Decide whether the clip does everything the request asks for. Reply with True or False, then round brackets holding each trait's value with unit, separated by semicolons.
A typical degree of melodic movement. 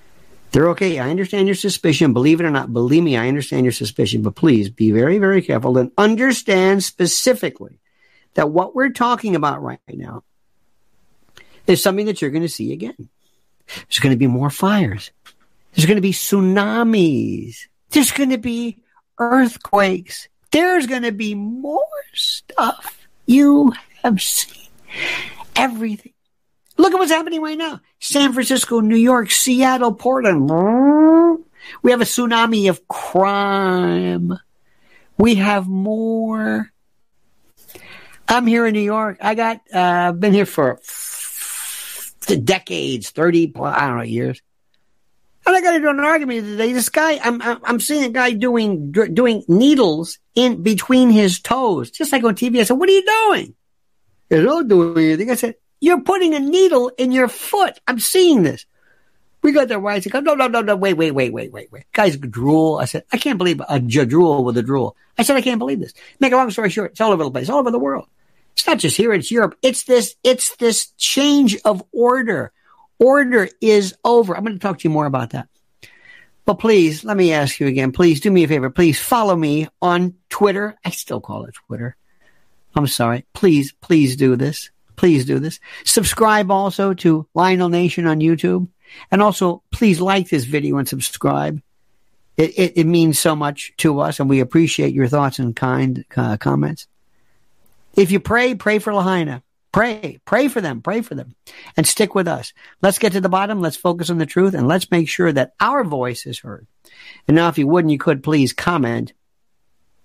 False (7.5 semitones)